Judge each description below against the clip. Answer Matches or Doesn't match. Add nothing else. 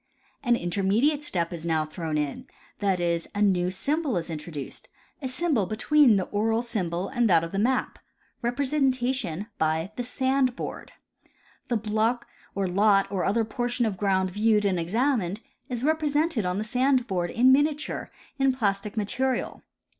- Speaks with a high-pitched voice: Matches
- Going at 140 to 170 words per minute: Matches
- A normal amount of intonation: Doesn't match